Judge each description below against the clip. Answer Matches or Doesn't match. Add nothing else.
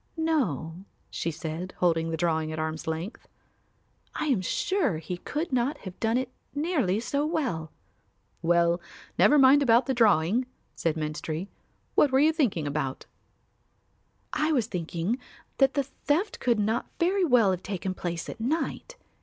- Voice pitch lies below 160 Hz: Doesn't match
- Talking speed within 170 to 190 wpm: Doesn't match